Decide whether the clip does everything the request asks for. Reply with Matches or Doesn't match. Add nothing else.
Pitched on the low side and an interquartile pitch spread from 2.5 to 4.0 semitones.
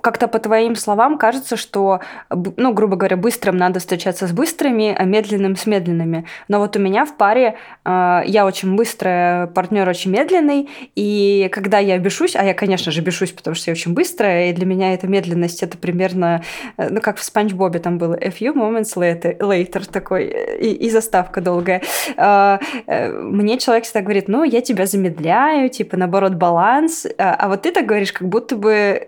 Doesn't match